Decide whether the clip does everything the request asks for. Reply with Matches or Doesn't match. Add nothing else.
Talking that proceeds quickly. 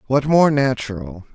Doesn't match